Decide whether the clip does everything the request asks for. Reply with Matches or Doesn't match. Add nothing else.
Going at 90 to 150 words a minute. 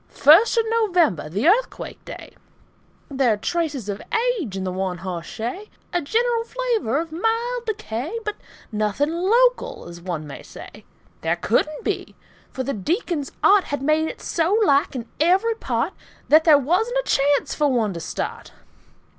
Doesn't match